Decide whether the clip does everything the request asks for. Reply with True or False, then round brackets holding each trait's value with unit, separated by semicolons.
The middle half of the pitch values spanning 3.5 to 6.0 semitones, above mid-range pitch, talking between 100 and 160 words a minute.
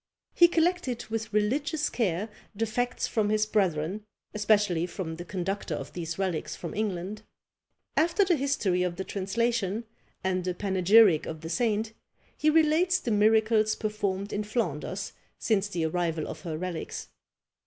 True (4.0 semitones; 210 Hz; 150 wpm)